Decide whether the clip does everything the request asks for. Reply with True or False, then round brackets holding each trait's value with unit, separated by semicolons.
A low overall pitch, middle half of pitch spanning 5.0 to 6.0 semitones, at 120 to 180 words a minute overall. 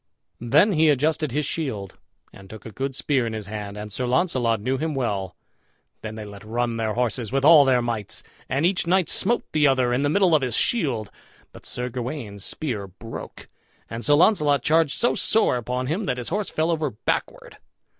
False (130 Hz; 5.4 semitones; 200 wpm)